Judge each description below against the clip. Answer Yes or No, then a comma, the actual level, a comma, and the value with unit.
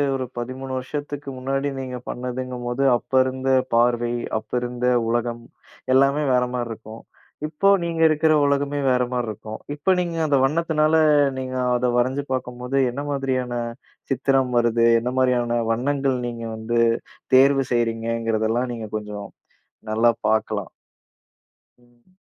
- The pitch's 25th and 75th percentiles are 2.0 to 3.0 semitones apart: Yes, narrow, 2.5 semitones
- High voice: No, low, 125 Hz